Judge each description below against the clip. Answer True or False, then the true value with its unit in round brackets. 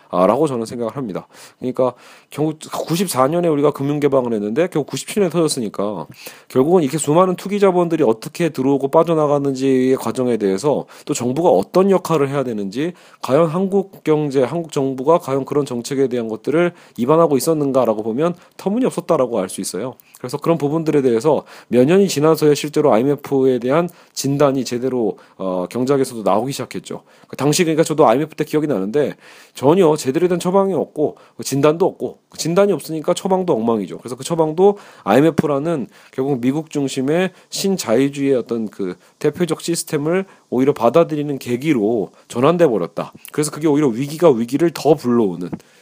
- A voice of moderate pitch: True (145 Hz)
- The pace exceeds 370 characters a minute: True (395 characters per minute)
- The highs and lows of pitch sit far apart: False (4.4 semitones)